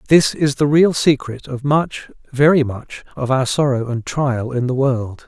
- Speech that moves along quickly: No, average, 195 wpm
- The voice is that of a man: Yes, male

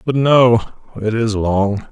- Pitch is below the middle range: Yes, low, 110 Hz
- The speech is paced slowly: Yes, slow, 125 wpm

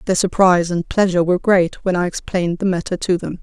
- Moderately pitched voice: Yes, medium, 180 Hz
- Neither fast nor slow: No, fast, 230 wpm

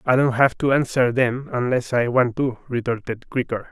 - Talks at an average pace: Yes, average, 195 wpm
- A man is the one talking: Yes, male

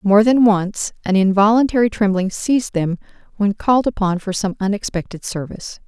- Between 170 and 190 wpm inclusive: No, average, 155 wpm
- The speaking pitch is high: Yes, high, 205 Hz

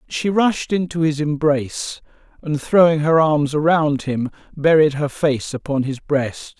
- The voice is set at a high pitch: No, medium, 150 Hz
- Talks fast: No, average, 155 wpm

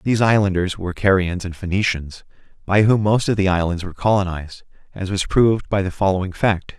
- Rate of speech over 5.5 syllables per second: Yes, 5.9 syllables/s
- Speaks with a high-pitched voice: No, very low, 95 Hz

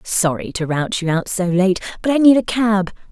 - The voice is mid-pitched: No, high, 195 Hz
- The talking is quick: Yes, fast, 230 wpm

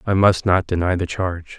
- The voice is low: Yes, very low, 90 Hz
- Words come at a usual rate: No, fast, 230 wpm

